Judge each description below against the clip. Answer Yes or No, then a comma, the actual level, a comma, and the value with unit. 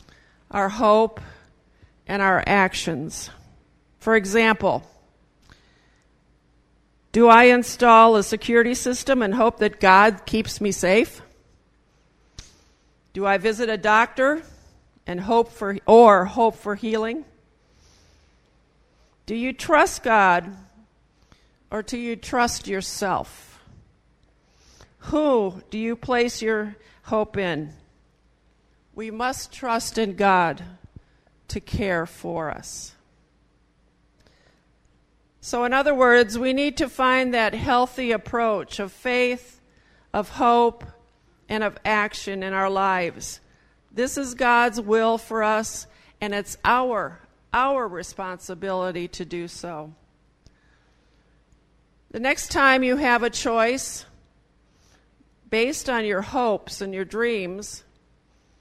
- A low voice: No, high, 220 Hz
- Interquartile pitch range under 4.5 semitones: Yes, average, 3.9 semitones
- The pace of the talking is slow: Yes, slow, 110 wpm